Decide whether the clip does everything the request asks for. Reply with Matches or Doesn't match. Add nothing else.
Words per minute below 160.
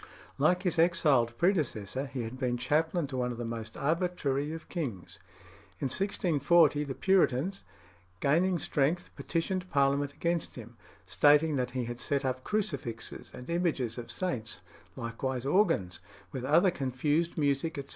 Matches